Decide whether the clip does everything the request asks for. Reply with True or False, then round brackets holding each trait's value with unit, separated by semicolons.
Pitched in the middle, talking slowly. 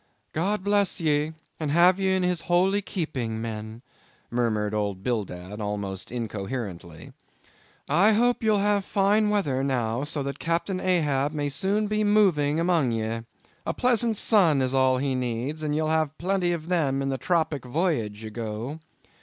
False (150 Hz; 160 wpm)